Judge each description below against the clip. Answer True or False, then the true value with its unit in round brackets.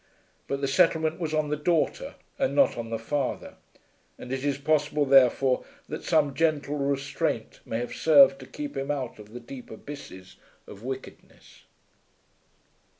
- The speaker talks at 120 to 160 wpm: True (155 wpm)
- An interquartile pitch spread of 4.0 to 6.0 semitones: False (3.3 semitones)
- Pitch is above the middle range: False (140 Hz)